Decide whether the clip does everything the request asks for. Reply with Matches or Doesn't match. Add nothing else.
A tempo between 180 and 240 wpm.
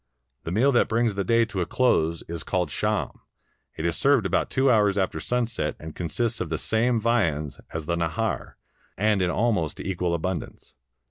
Matches